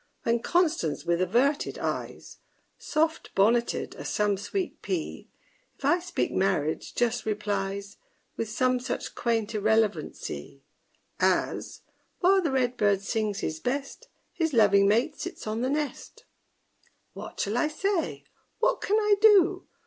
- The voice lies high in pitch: Yes, high, 235 Hz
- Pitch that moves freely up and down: Yes, wide, 8.0 semitones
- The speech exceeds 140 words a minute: No, slow, 135 wpm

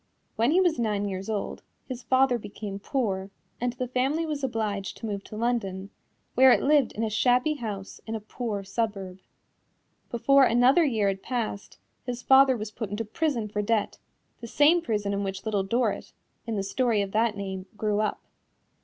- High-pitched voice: Yes, high, 225 Hz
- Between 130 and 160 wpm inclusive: No, average, 185 wpm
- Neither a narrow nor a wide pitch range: Yes, average, 3.9 semitones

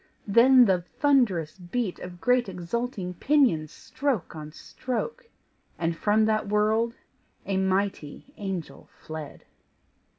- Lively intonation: Yes, wide, 5.8 semitones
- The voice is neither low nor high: No, high, 205 Hz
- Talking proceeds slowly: Yes, slow, 110 wpm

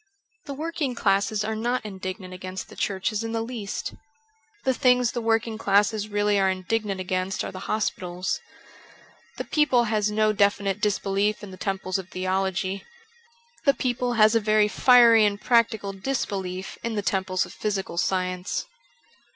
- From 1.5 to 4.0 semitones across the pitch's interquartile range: Yes, average, 3.0 semitones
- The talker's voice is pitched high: Yes, high, 205 Hz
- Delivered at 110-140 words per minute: No, average, 160 wpm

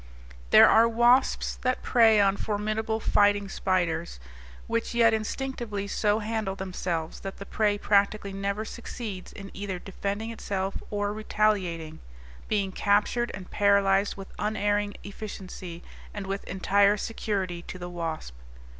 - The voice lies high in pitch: Yes, high, 205 Hz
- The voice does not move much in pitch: Yes, narrow, 2.0 semitones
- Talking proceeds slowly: Yes, slow, 130 wpm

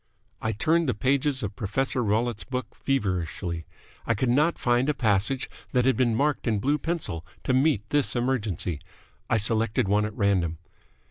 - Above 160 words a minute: Yes, average, 170 wpm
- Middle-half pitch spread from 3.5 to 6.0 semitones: Yes, average, 4.6 semitones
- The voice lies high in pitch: No, low, 120 Hz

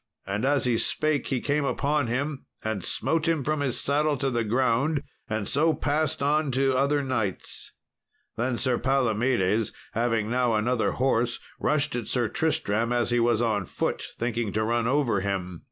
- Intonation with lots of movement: No, average, 3.9 semitones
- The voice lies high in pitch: No, low, 125 Hz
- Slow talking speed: No, average, 170 wpm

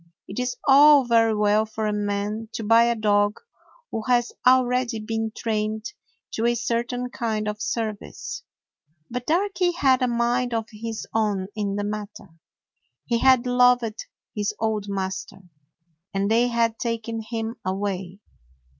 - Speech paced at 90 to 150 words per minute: Yes, average, 145 wpm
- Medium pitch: No, high, 225 Hz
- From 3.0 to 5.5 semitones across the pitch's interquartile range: No, narrow, 2.5 semitones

